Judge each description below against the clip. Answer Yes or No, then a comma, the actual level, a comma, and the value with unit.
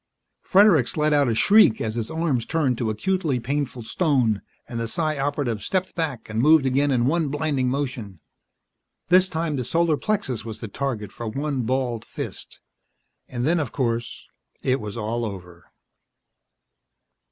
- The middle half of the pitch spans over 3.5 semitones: Yes, average, 5.0 semitones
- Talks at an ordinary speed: Yes, average, 160 wpm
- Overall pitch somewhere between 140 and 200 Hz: No, low, 130 Hz